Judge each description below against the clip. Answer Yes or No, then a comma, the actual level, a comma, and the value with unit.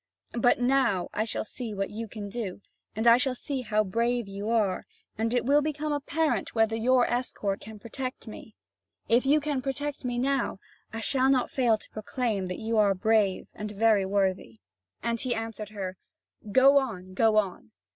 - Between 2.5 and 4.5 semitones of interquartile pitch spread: Yes, average, 3.6 semitones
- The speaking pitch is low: No, high, 225 Hz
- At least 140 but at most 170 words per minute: No, average, 185 wpm